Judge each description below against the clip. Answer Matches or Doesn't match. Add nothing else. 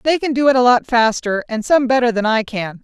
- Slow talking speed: Doesn't match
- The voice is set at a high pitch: Matches